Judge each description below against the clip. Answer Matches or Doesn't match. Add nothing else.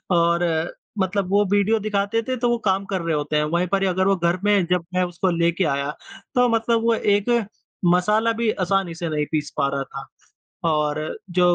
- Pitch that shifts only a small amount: Doesn't match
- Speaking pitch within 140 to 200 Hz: Matches